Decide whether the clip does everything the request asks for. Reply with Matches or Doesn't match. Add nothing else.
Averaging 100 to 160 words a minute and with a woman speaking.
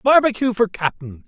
Doesn't match